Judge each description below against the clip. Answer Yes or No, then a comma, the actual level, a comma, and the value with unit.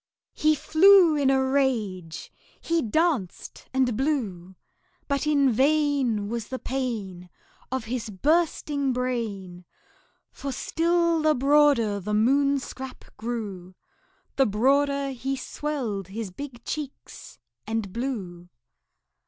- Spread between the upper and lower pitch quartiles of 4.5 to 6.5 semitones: Yes, average, 5.2 semitones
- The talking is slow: Yes, slow, 110 wpm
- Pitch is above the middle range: Yes, very high, 260 Hz